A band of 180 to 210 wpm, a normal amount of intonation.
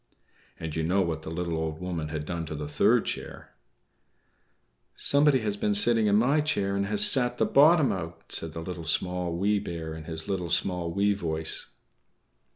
Yes: average, 185 wpm; average, 4.2 semitones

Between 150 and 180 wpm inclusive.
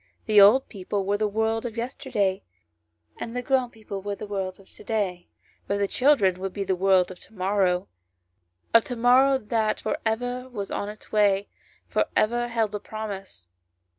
No: average, 190 wpm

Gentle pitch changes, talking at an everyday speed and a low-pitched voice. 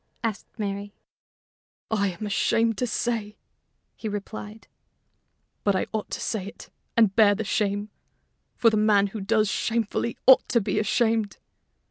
No: narrow, 1.9 semitones; average, 145 wpm; high, 215 Hz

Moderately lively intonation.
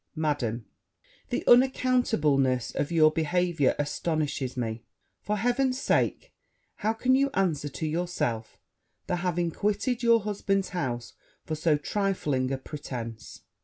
No: wide, 7.0 semitones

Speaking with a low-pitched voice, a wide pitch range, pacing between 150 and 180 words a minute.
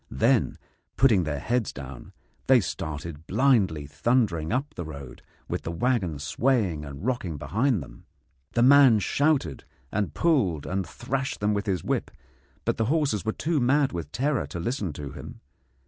Yes: low, 100 Hz; wide, 8.7 semitones; average, 165 wpm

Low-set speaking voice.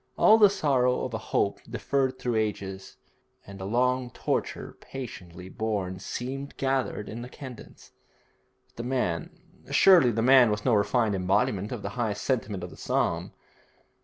Yes: low, 115 Hz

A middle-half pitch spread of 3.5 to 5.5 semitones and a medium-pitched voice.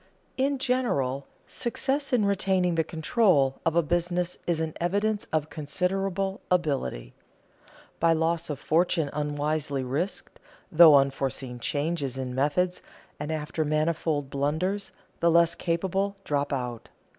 Yes: average, 4.1 semitones; medium, 160 Hz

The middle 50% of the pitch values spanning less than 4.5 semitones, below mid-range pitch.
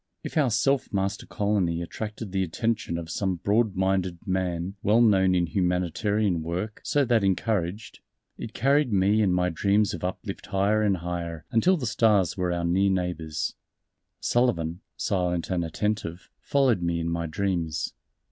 Yes: average, 3.6 semitones; very low, 95 Hz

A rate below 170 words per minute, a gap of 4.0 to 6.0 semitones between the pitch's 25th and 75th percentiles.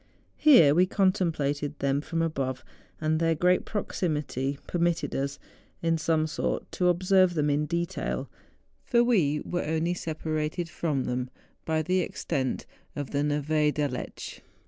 No: average, 140 wpm; average, 3.2 semitones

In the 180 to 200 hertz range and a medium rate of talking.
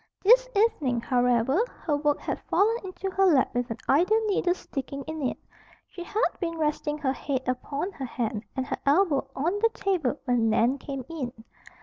No: very high, 290 Hz; average, 185 wpm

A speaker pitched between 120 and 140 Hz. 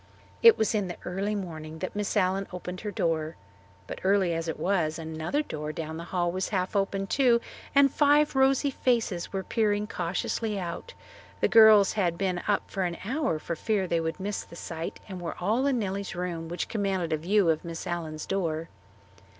No: medium, 185 Hz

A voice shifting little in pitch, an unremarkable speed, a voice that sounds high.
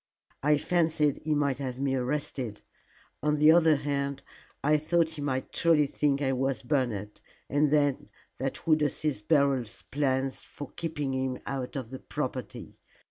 No: narrow, 2.2 semitones; average, 155 wpm; medium, 140 Hz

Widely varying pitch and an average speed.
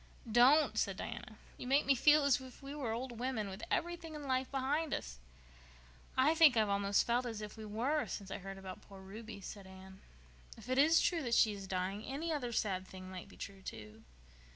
No: wide, 6.0 semitones; fast, 215 wpm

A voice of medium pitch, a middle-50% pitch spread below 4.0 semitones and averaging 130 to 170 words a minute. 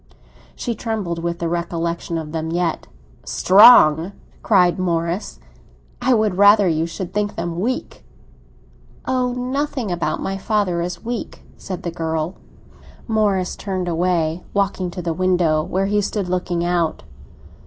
Yes: medium, 180 Hz; average, 3.4 semitones; average, 140 wpm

